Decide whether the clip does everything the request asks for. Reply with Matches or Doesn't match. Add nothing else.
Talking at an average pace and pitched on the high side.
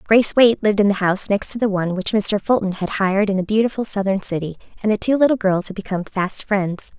Doesn't match